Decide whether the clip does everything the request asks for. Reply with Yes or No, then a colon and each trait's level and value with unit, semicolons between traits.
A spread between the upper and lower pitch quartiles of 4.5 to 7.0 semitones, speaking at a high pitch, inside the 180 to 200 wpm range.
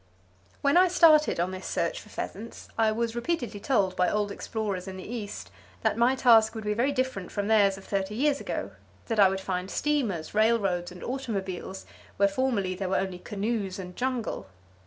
No: average, 4.0 semitones; high, 210 Hz; average, 185 wpm